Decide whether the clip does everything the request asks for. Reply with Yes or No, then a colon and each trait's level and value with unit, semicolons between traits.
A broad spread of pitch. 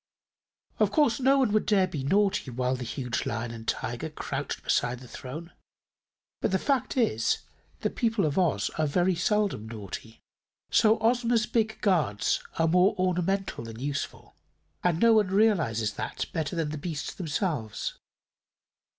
Yes: wide, 8.6 semitones